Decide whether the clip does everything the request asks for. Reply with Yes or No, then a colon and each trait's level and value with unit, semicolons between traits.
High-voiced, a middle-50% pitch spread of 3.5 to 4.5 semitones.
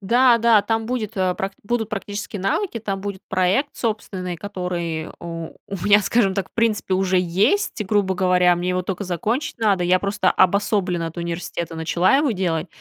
No: high, 195 Hz; average, 3.1 semitones